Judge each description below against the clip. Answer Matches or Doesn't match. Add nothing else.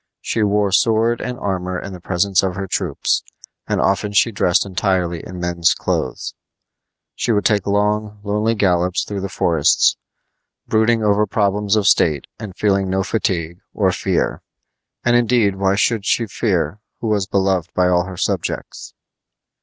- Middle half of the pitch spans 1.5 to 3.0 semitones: Matches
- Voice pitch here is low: Matches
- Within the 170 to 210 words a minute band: Doesn't match